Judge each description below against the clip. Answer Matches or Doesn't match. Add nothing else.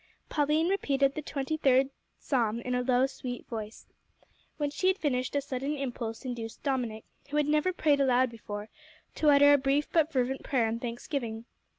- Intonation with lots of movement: Doesn't match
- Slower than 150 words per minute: Doesn't match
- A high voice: Matches